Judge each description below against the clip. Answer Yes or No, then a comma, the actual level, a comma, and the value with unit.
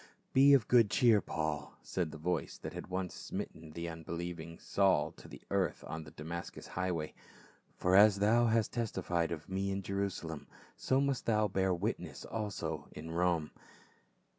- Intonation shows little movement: No, average, 3.9 semitones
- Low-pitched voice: Yes, very low, 95 Hz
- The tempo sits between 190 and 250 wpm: No, average, 165 wpm